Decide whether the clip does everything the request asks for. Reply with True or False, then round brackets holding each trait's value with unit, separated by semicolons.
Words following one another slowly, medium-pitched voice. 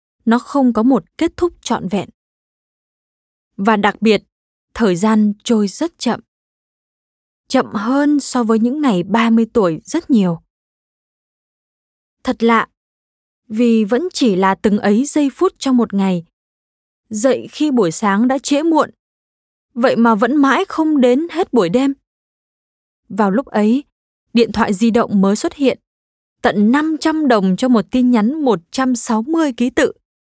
False (150 wpm; 235 Hz)